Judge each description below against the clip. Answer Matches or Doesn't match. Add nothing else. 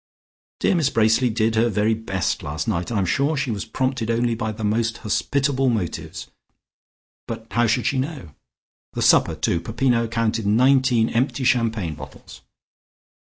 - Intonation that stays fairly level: Doesn't match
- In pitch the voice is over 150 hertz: Doesn't match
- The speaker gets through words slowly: Doesn't match